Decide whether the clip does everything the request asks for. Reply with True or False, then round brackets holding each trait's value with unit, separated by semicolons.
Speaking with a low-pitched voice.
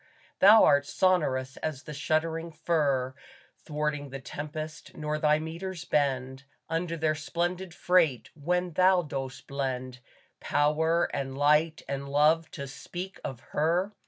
False (155 Hz)